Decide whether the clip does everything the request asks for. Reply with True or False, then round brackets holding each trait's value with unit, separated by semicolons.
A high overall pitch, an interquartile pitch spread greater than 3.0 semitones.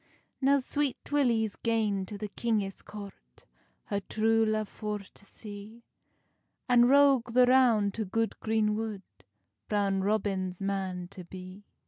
False (215 Hz; 2.7 semitones)